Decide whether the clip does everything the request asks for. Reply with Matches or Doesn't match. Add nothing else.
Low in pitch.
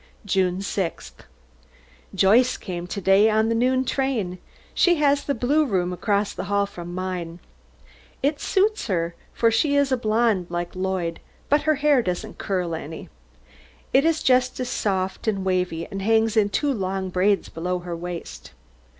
Doesn't match